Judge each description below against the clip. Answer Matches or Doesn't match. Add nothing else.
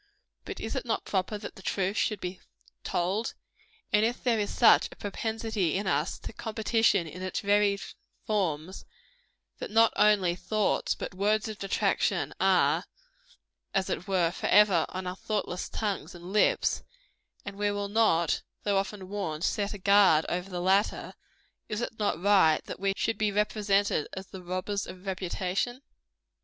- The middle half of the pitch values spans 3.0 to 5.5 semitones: Doesn't match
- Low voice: Doesn't match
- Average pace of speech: Matches